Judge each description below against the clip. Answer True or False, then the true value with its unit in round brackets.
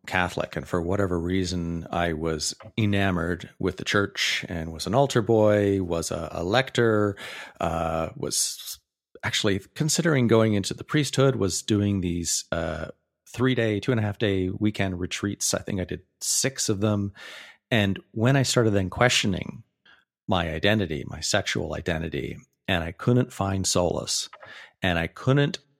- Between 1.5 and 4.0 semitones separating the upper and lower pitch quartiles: False (4.4 semitones)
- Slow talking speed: False (155 wpm)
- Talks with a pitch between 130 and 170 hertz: False (100 Hz)